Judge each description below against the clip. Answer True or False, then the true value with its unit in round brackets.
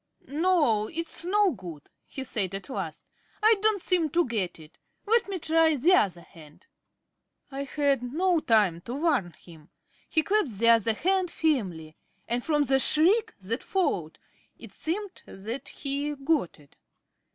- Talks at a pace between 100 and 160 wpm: True (155 wpm)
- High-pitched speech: True (275 Hz)